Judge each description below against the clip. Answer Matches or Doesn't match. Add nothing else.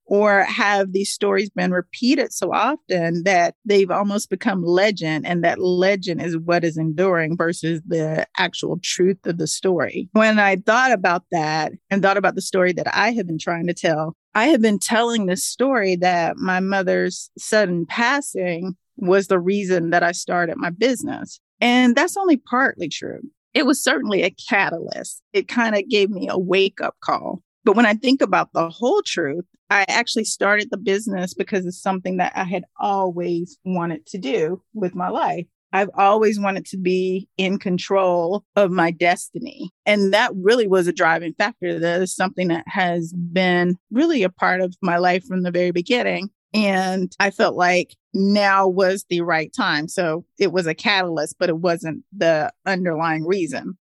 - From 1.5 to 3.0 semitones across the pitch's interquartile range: Matches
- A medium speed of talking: Matches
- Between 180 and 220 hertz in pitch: Matches